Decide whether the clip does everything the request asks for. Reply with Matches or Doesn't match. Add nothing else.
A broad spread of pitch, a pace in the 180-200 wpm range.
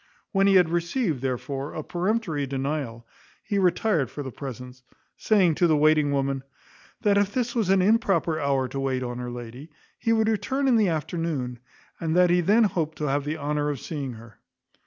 Matches